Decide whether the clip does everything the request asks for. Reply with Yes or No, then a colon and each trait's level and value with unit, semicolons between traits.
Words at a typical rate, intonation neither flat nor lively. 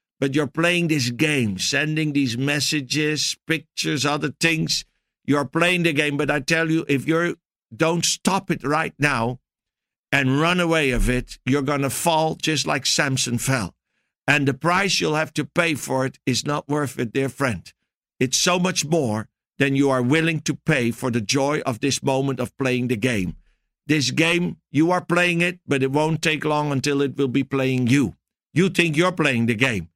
Yes: average, 195 wpm; average, 3.4 semitones